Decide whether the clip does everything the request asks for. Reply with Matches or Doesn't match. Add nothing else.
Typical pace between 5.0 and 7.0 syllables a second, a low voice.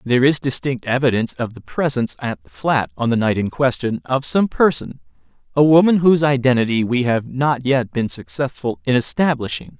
Matches